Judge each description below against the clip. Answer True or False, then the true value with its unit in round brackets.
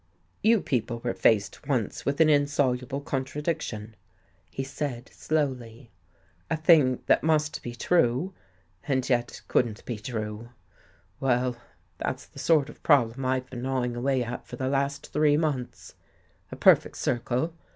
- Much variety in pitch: False (3.2 semitones)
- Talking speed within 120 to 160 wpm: True (150 wpm)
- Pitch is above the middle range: False (130 Hz)